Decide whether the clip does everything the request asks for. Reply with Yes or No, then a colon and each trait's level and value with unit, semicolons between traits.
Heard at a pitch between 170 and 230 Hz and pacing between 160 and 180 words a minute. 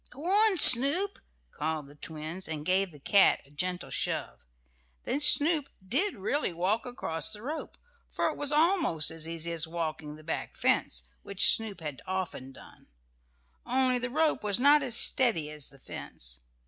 Yes: high, 190 Hz; average, 170 wpm